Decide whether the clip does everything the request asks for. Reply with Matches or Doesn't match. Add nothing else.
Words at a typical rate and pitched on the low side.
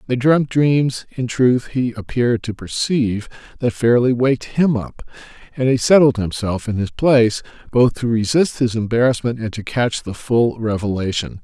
Matches